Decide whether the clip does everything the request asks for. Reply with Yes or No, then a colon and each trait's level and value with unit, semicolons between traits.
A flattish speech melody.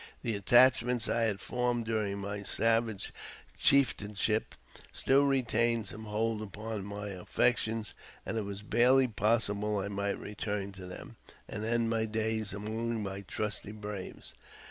Yes: narrow, 2.2 semitones